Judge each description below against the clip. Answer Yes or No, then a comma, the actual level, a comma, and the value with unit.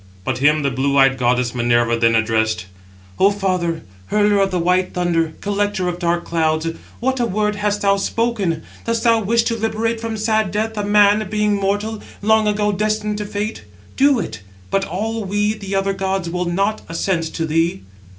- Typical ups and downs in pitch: Yes, average, 4.3 semitones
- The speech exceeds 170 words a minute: Yes, average, 185 wpm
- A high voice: Yes, high, 195 Hz